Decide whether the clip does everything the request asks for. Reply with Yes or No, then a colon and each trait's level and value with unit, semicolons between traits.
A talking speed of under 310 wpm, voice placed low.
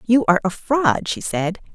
No: fast, 205 wpm; high, 210 Hz